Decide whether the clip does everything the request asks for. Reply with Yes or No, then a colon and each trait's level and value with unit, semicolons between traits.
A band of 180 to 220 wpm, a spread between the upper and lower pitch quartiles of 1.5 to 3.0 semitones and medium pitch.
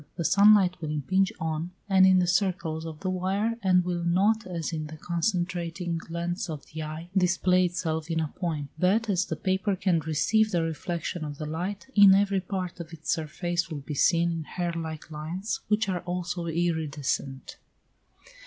Yes: average, 185 wpm; average, 2.7 semitones; medium, 175 Hz